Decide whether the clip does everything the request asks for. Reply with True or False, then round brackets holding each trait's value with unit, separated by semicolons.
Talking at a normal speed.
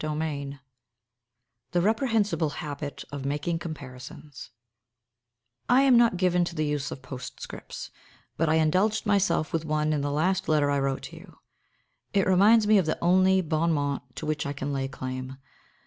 True (165 wpm)